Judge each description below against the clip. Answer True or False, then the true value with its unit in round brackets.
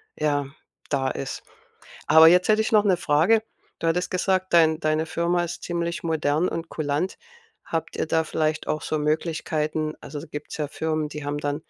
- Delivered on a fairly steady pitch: True (2.2 semitones)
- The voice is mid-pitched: True (160 Hz)